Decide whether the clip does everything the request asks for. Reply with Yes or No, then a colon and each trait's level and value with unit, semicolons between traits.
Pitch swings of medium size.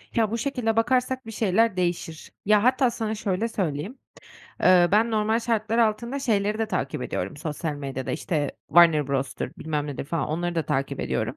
No: wide, 6.1 semitones